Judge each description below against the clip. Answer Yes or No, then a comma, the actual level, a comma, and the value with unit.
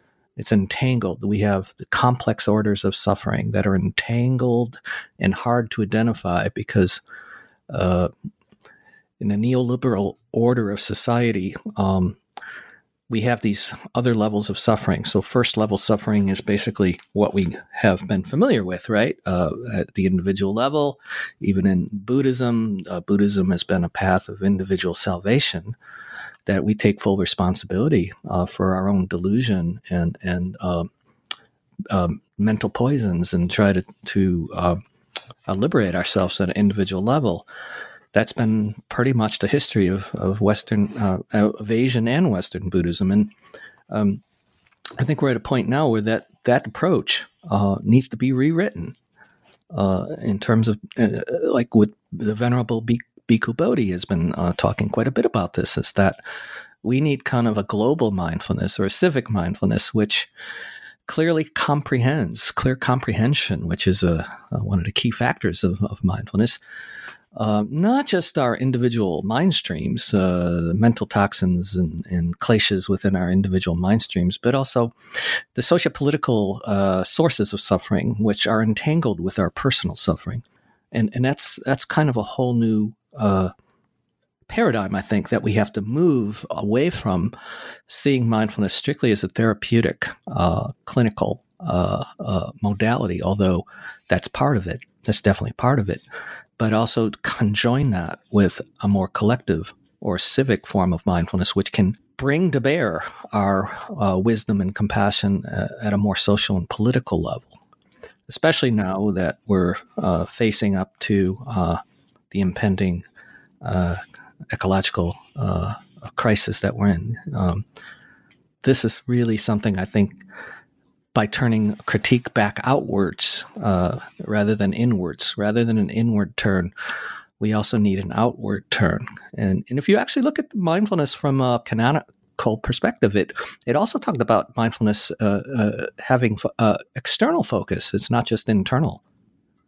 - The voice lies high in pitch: No, low, 105 Hz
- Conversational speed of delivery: Yes, average, 150 wpm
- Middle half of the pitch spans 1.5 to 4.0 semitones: Yes, average, 3.7 semitones